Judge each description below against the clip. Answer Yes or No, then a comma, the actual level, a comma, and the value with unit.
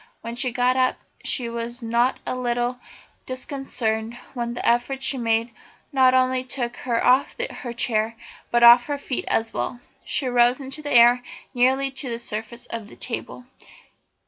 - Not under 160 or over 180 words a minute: Yes, average, 170 wpm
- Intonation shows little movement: Yes, narrow, 1.6 semitones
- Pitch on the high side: Yes, high, 245 Hz